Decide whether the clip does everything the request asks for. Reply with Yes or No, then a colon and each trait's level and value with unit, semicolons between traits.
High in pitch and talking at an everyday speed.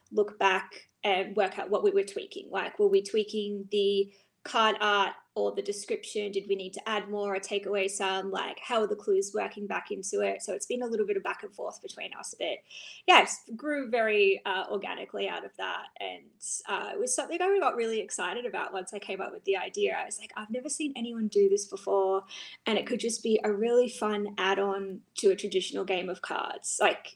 No: high, 215 Hz; fast, 230 wpm